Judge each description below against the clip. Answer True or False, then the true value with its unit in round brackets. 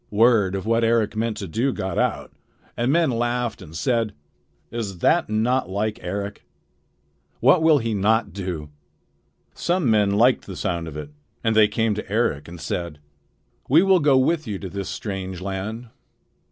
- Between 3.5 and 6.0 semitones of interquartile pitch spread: True (3.9 semitones)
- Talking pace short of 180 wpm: True (170 wpm)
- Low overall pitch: True (110 Hz)